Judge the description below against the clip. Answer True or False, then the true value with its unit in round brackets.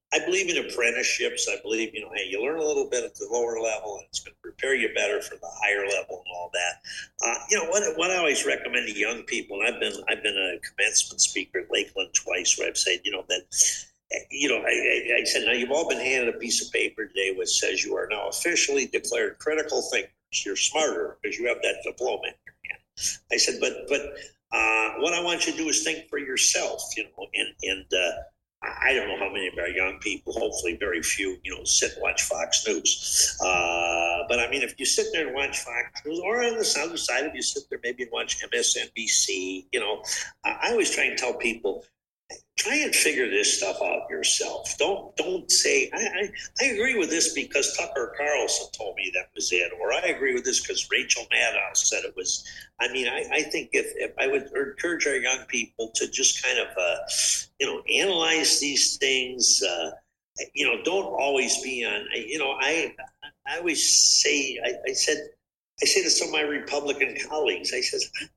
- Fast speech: True (220 wpm)